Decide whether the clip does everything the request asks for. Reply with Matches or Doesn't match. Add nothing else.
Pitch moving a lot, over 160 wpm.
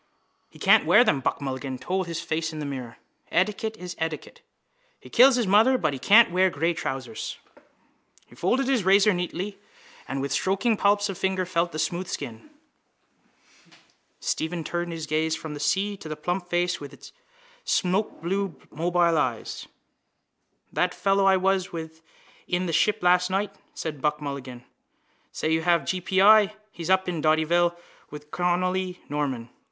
Doesn't match